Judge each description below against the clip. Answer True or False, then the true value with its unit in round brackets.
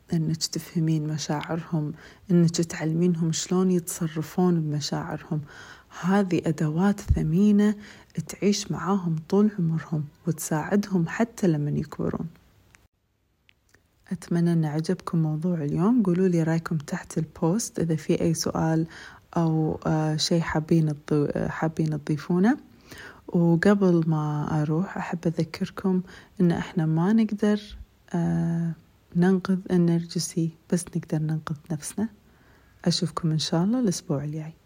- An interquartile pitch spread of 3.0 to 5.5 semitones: False (2.6 semitones)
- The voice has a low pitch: False (170 Hz)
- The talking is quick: False (105 wpm)